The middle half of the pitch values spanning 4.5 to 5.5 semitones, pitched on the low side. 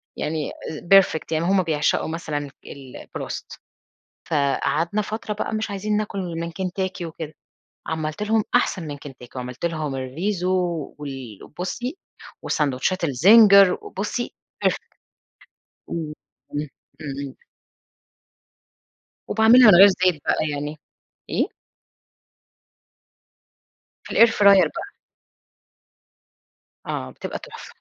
No: average, 5.2 semitones; medium, 170 Hz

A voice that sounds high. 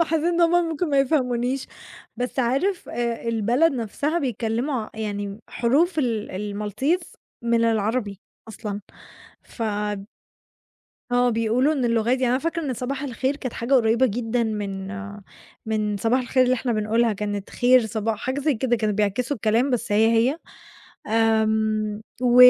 Yes: high, 235 Hz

